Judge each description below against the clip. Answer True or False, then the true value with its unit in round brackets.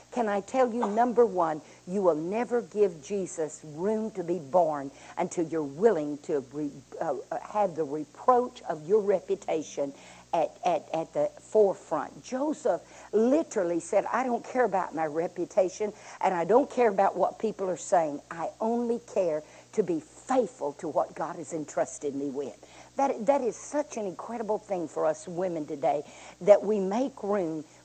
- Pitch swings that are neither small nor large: False (6.0 semitones)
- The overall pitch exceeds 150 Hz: True (190 Hz)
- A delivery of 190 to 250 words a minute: False (170 wpm)